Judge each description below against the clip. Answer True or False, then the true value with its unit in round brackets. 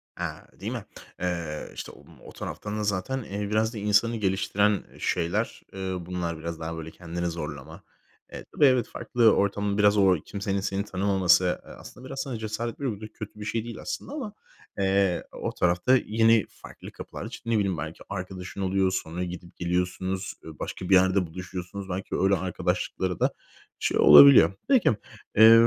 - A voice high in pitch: False (95 Hz)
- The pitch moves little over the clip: False (3.1 semitones)